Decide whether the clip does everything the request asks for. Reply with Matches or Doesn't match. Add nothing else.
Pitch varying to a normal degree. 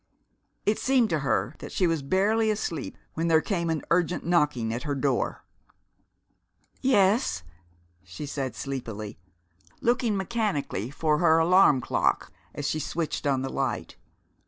Doesn't match